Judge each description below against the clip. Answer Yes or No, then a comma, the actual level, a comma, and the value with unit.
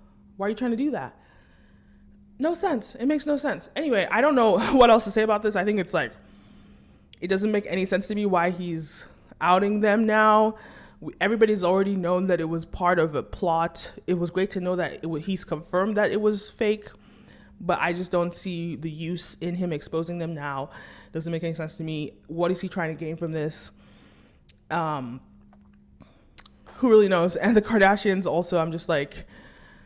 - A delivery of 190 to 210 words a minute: Yes, average, 200 wpm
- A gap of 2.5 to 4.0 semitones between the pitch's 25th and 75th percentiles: No, average, 4.4 semitones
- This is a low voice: No, medium, 180 Hz